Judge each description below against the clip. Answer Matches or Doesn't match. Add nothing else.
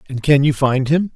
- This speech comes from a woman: Doesn't match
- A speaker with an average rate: Doesn't match